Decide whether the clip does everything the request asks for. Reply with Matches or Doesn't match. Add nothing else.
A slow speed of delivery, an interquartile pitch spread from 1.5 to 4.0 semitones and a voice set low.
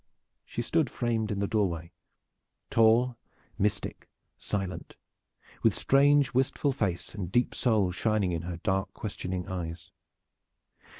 Doesn't match